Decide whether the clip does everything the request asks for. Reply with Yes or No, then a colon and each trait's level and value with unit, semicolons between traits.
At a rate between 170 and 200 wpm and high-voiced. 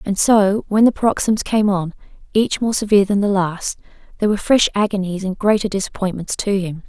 Yes: average, 190 wpm; high, 200 Hz